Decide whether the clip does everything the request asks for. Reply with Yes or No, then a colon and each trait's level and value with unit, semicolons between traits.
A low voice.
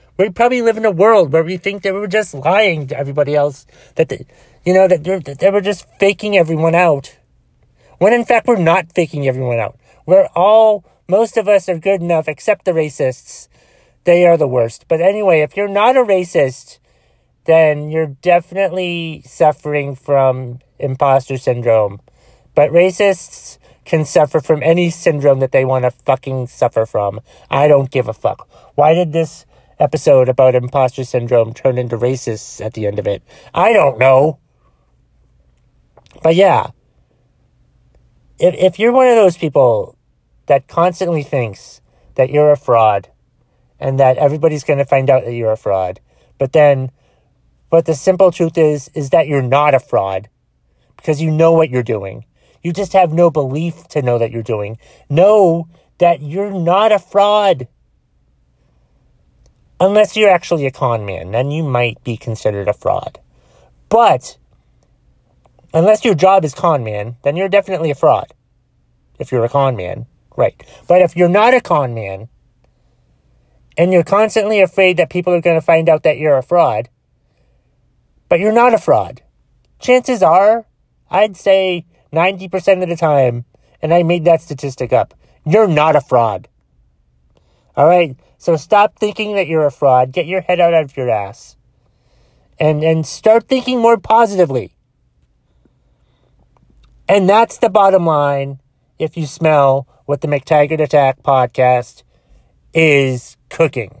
No: medium, 155 Hz